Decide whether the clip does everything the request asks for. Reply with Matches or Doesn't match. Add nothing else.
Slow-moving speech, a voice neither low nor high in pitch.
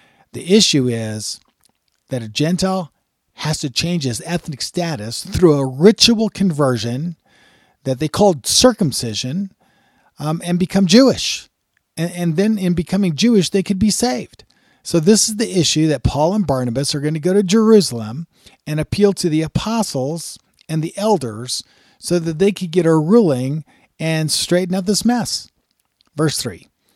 Doesn't match